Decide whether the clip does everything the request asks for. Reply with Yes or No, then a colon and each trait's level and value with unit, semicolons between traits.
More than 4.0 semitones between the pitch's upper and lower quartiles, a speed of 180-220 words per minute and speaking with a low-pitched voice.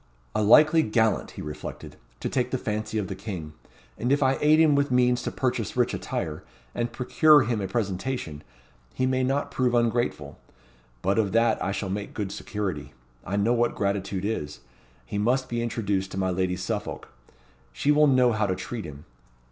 Yes: average, 4.7 semitones; average, 190 wpm; low, 110 Hz